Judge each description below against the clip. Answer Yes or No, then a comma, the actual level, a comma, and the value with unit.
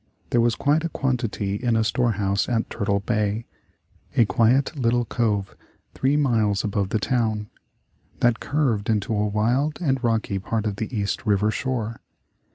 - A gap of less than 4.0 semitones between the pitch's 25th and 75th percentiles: Yes, average, 3.0 semitones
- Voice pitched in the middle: No, low, 115 Hz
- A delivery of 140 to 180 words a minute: Yes, average, 160 wpm